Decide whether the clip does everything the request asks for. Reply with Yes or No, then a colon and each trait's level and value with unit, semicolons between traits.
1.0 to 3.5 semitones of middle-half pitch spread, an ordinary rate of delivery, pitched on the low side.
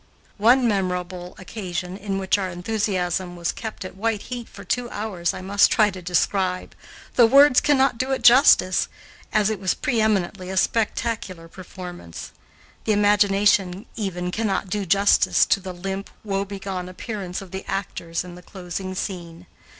No: average, 2.8 semitones; average, 160 wpm; high, 195 Hz